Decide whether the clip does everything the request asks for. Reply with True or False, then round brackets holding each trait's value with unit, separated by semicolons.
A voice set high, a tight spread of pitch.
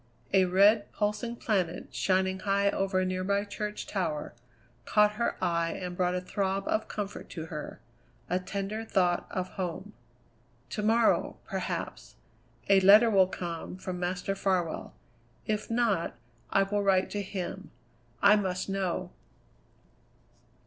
True (195 Hz; 2.2 semitones)